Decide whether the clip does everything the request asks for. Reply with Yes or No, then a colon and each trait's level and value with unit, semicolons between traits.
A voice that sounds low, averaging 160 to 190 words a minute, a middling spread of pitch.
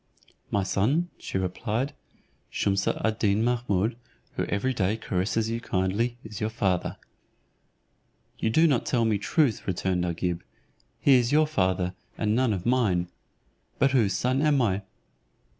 No: low, 110 Hz; average, 150 wpm; average, 4.5 semitones